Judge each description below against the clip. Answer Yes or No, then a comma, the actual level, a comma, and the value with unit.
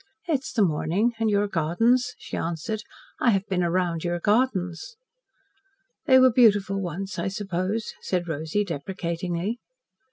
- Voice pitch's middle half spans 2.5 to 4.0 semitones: No, average, 4.5 semitones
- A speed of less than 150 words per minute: Yes, average, 140 wpm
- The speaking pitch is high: Yes, high, 195 Hz